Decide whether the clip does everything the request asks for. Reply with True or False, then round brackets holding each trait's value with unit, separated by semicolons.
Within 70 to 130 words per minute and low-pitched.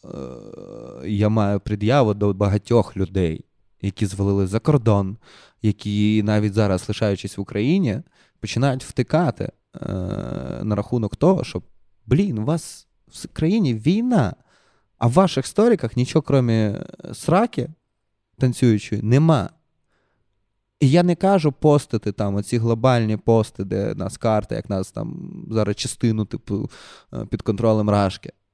True (120 wpm; 110 Hz)